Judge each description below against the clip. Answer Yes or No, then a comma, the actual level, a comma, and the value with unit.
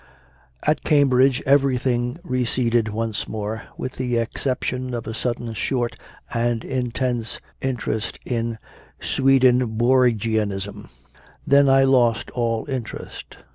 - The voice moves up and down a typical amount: No, narrow, 2.2 semitones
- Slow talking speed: Yes, slow, 105 wpm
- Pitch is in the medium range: No, low, 120 Hz